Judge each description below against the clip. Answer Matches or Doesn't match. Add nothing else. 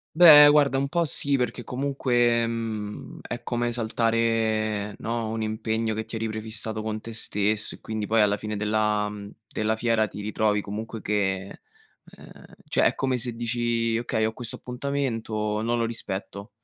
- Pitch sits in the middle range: Doesn't match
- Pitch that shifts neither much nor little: Doesn't match